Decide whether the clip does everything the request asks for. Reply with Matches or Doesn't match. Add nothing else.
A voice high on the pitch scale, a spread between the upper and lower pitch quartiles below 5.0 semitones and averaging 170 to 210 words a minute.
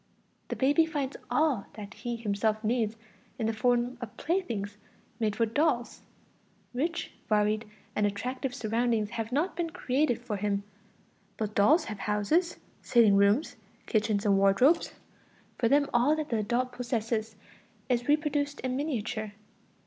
Doesn't match